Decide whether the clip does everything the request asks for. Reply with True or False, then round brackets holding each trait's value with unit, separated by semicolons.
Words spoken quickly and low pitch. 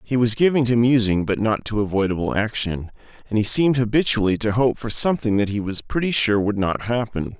True (210 wpm; 115 Hz)